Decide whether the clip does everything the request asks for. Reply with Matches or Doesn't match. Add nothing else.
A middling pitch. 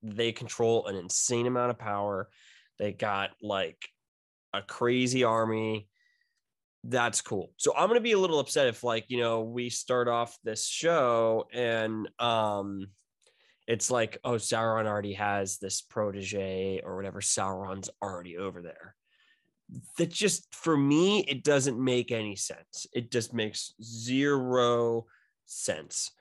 Doesn't match